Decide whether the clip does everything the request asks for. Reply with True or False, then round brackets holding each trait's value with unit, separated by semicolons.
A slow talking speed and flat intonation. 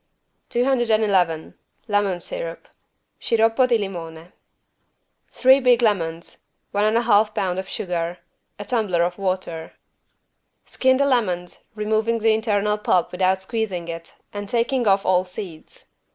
False (130 wpm; 4.2 semitones)